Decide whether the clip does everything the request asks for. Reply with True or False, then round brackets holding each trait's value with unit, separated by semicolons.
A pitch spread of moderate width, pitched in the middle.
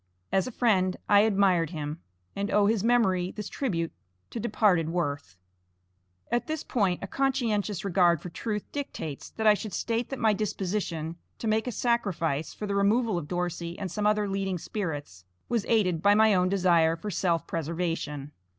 False (4.3 semitones; 195 Hz)